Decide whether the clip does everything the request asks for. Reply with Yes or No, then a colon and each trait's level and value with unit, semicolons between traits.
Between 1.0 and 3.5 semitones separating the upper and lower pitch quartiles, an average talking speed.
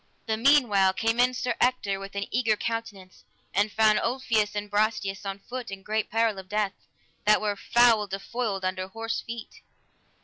Yes: average, 2.7 semitones; average, 170 wpm